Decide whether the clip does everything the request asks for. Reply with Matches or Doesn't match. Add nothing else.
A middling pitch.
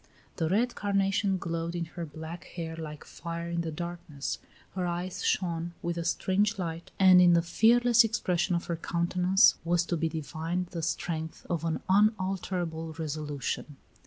Matches